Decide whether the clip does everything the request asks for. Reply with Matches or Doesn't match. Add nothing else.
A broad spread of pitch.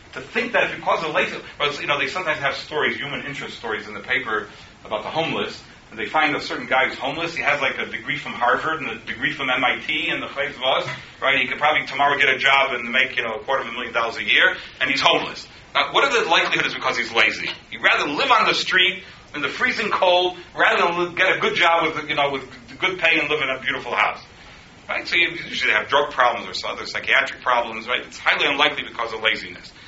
Doesn't match